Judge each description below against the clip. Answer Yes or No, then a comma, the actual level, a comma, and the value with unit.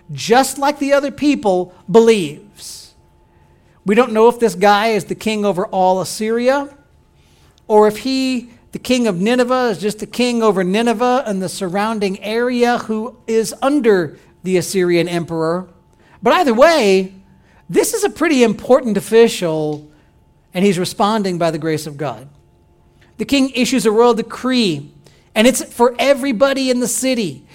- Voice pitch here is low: No, high, 220 Hz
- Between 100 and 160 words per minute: Yes, average, 155 wpm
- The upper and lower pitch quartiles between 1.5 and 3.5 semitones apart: No, average, 5.2 semitones